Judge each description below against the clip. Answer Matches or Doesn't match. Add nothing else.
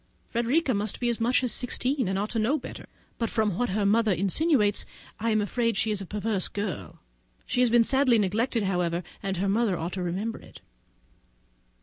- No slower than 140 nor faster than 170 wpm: Doesn't match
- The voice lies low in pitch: Doesn't match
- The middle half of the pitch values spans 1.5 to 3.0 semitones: Doesn't match